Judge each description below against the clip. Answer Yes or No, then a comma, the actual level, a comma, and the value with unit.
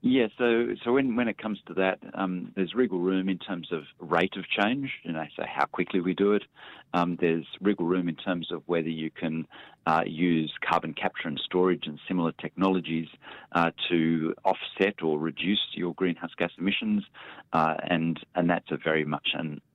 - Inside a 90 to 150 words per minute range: No, average, 190 wpm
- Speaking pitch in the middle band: No, very low, 85 Hz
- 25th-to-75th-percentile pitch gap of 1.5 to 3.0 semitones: Yes, narrow, 2.6 semitones